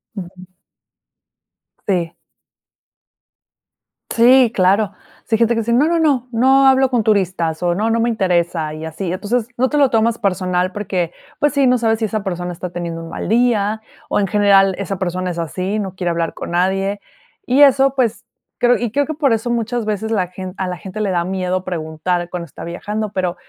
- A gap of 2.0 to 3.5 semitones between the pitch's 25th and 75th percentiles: No, average, 4.6 semitones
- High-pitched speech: Yes, high, 200 Hz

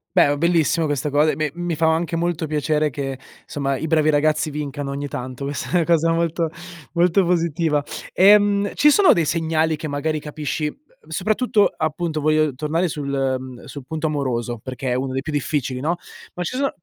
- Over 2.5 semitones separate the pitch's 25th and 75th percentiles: Yes, average, 2.9 semitones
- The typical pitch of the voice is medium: Yes, medium, 155 Hz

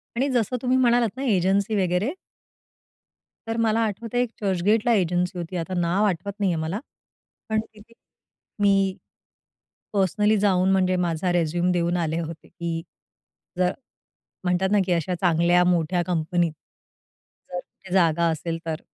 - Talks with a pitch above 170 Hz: Yes, medium, 185 Hz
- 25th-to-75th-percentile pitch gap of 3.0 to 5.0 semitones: Yes, average, 3.3 semitones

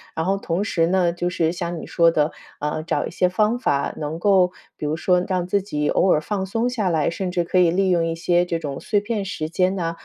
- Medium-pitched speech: Yes, medium, 175 Hz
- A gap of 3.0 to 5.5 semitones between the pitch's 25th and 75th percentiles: No, narrow, 2.6 semitones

